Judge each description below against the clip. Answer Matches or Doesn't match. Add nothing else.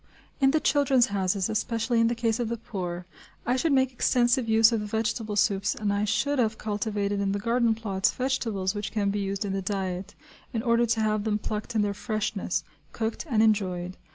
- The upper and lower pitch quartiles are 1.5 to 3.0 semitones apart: Matches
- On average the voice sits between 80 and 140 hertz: Doesn't match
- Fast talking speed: Matches